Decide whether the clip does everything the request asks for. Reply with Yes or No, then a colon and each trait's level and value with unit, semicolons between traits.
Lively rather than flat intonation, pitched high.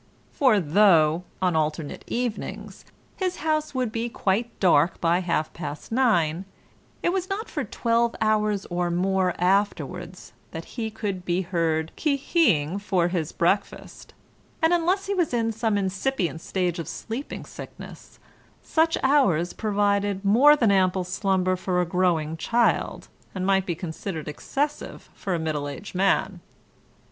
No: average, 5.0 semitones; high, 195 Hz